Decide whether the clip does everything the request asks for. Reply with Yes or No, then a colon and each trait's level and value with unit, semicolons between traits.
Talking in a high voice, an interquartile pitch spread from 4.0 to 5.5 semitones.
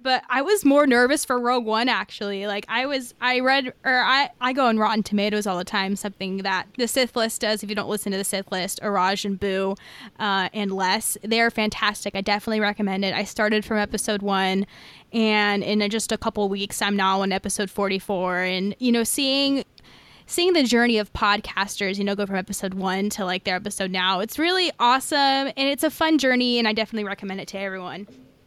No: high, 210 Hz; average, 3.6 semitones